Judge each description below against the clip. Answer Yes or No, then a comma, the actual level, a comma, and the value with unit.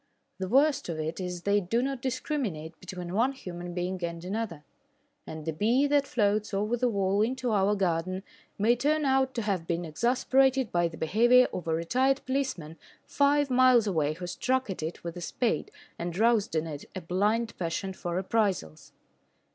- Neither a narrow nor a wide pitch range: No, wide, 6.4 semitones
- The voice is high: Yes, high, 200 Hz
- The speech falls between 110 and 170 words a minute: No, average, 180 wpm